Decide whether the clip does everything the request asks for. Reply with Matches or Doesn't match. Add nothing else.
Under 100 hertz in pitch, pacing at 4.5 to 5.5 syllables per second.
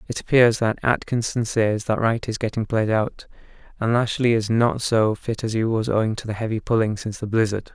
Doesn't match